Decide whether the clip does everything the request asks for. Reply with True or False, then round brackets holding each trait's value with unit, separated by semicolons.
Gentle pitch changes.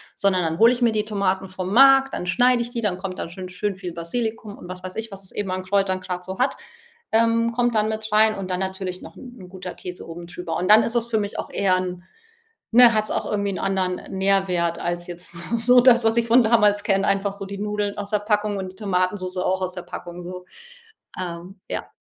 False (3.1 semitones)